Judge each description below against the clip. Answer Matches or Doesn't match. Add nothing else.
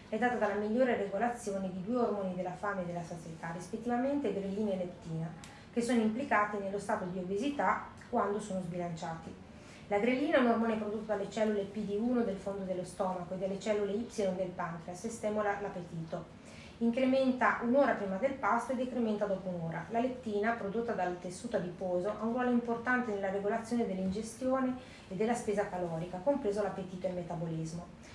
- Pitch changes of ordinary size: Matches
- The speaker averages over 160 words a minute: Matches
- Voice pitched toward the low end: Doesn't match